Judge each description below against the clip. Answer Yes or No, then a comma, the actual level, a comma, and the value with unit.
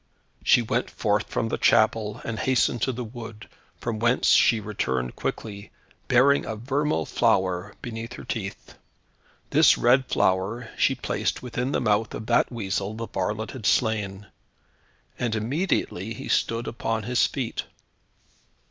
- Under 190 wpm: Yes, average, 145 wpm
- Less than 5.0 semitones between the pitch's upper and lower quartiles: Yes, average, 2.7 semitones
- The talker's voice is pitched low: Yes, low, 115 Hz